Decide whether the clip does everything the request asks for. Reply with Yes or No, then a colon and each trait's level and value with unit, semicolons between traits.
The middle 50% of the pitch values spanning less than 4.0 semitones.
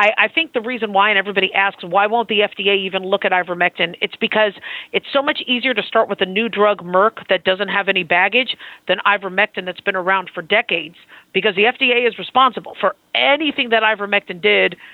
Yes: average, 2.9 semitones